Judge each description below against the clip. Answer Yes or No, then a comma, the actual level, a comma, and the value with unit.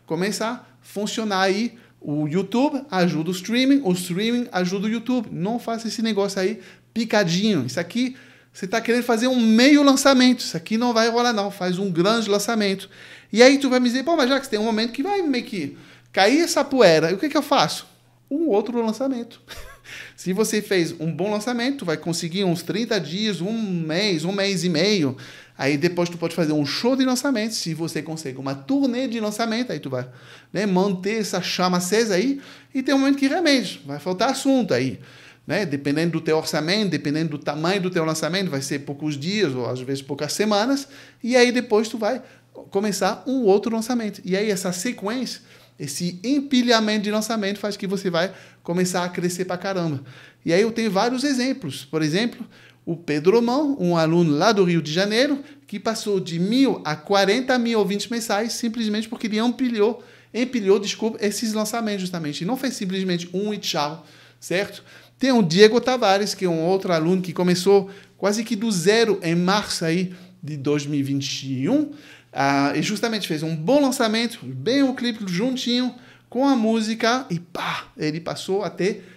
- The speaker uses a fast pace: Yes, fast, 190 wpm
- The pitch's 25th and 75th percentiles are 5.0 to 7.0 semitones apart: Yes, average, 5.3 semitones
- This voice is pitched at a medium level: No, high, 205 Hz